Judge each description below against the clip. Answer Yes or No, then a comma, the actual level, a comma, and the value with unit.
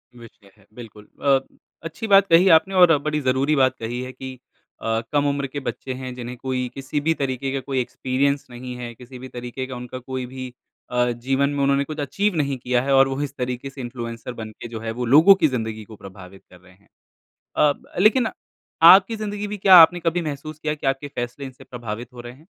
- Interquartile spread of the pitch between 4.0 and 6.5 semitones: No, average, 3.4 semitones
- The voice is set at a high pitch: No, low, 130 Hz